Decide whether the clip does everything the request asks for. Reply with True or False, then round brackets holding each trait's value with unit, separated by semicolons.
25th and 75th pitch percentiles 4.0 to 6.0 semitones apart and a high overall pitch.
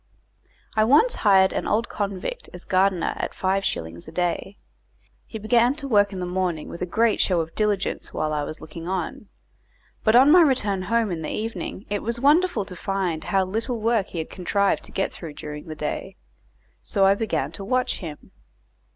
True (4.3 semitones; 195 Hz)